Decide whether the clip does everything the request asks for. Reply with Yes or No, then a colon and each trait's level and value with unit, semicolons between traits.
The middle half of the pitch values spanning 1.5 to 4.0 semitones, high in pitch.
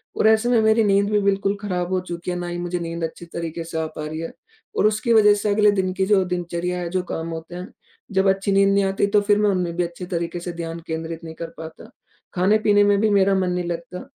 No: average, 3.0 semitones; medium, 180 Hz